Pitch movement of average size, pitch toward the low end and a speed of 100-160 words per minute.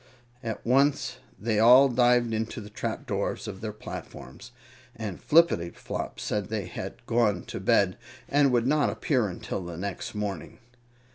Yes: average, 3.6 semitones; low, 110 Hz; average, 150 wpm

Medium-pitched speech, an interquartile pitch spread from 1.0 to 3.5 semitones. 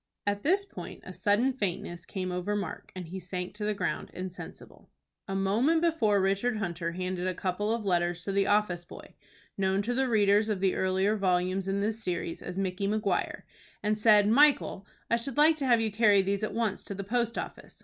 No: high, 200 Hz; average, 2.9 semitones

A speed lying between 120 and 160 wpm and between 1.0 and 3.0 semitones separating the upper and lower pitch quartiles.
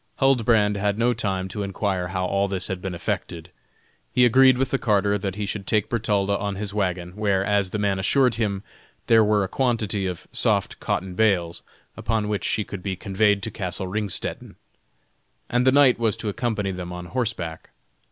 No: average, 190 wpm; average, 2.7 semitones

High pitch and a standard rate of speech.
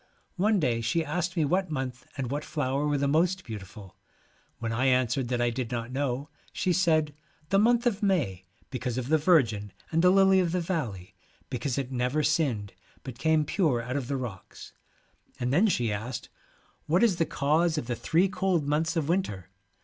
No: medium, 140 Hz; average, 195 wpm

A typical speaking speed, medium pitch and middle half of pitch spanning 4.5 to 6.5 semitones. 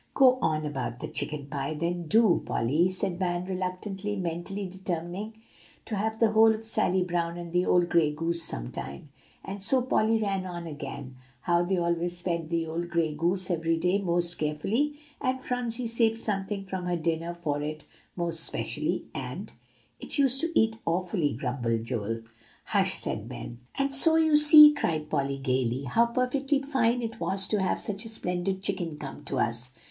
Yes: average, 180 wpm; medium, 175 Hz; wide, 5.6 semitones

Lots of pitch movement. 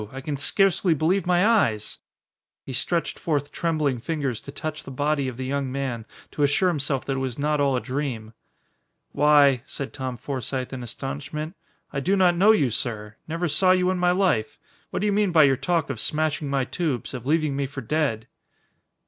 No: average, 3.9 semitones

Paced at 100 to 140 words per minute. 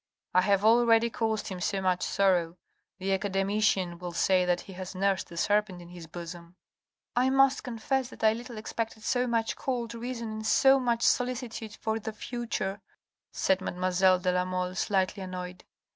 No: average, 175 wpm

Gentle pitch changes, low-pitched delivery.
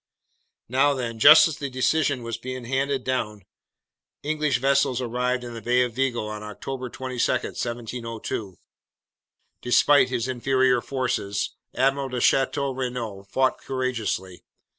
Yes: narrow, 2.3 semitones; low, 125 Hz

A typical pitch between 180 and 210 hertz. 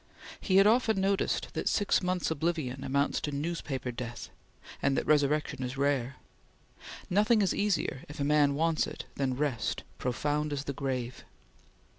No: medium, 145 Hz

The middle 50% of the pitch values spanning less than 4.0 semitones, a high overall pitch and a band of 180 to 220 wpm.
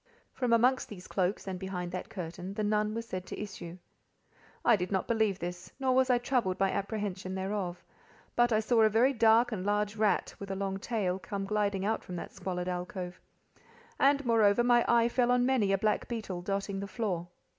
Yes: average, 3.6 semitones; high, 205 Hz; average, 200 wpm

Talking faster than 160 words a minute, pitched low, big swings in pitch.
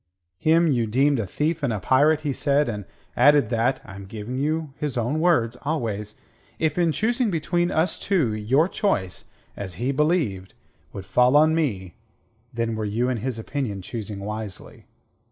Yes: average, 170 wpm; low, 130 Hz; wide, 6.4 semitones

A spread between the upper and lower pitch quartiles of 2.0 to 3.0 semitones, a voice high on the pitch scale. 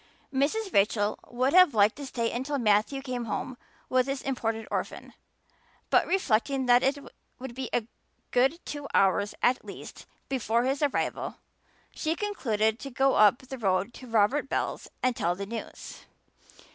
No: average, 3.7 semitones; very high, 250 Hz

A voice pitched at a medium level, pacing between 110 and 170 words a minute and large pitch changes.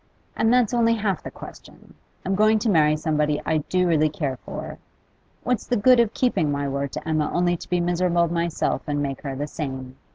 No: medium, 170 Hz; fast, 205 wpm; wide, 5.7 semitones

